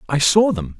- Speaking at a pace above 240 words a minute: No, fast, 225 wpm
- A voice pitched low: Yes, low, 120 Hz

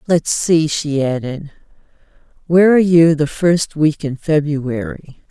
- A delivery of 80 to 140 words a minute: Yes, slow, 135 wpm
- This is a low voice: No, medium, 155 Hz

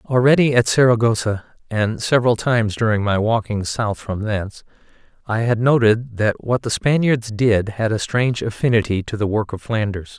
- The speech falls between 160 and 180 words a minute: Yes, average, 170 wpm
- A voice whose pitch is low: Yes, low, 110 Hz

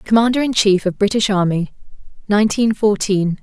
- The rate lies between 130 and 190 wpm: Yes, average, 140 wpm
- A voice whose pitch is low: No, high, 205 Hz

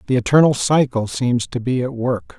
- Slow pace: No, average, 200 wpm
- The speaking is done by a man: Yes, male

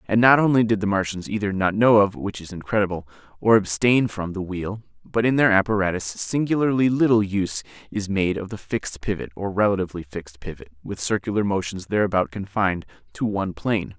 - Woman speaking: No, male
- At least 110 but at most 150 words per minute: No, average, 185 wpm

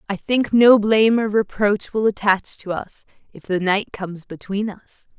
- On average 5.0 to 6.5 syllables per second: No, 4.6 syllables/s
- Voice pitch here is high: Yes, high, 205 Hz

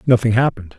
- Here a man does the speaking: Yes, male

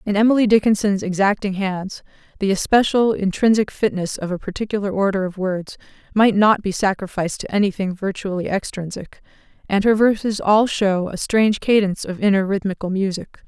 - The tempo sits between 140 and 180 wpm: Yes, average, 155 wpm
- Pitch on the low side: No, high, 200 Hz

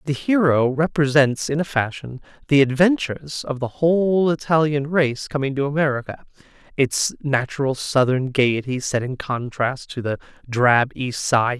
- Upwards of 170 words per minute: No, average, 145 wpm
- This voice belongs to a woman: No, male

